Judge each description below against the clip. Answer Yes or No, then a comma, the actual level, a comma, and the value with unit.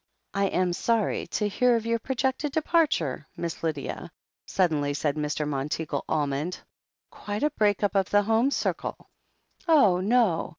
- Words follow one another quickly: No, average, 145 wpm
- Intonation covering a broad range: Yes, wide, 7.1 semitones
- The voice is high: Yes, high, 195 Hz